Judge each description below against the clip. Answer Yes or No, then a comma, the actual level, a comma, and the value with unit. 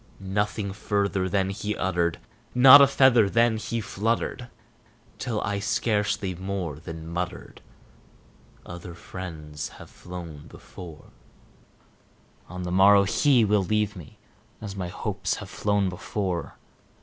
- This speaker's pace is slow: Yes, slow, 125 wpm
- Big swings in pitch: No, average, 3.1 semitones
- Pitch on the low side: Yes, low, 100 Hz